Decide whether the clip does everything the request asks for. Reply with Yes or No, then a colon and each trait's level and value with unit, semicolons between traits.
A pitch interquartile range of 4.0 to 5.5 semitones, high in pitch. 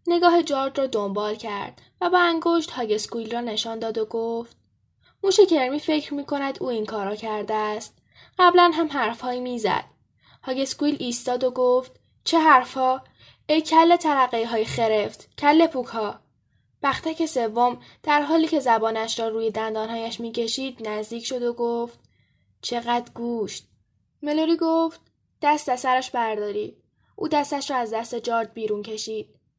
Yes: average, 4.7 semitones; high, 245 Hz